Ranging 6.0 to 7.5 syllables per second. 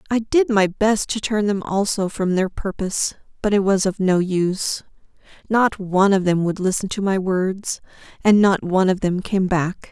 No: 4.8 syllables/s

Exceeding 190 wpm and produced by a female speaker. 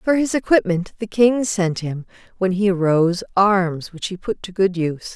Yes: average, 200 wpm; female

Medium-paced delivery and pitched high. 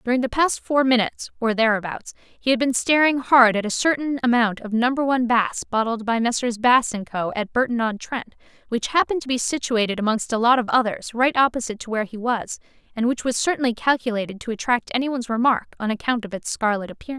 No: fast, 215 wpm; high, 240 Hz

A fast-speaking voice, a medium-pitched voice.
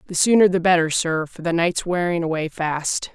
Yes: fast, 210 wpm; medium, 170 Hz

